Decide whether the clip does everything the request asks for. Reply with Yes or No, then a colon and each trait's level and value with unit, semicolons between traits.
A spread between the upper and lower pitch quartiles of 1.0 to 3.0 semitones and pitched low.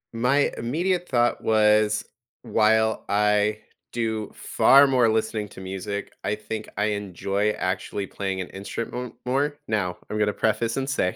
Yes: narrow, 2.6 semitones; low, 110 Hz